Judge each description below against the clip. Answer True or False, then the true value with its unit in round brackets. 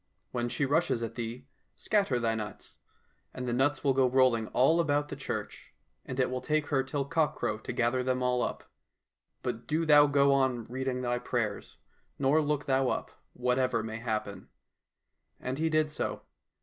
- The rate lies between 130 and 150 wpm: False (175 wpm)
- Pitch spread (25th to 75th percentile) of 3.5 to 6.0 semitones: False (3.0 semitones)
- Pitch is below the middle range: True (130 Hz)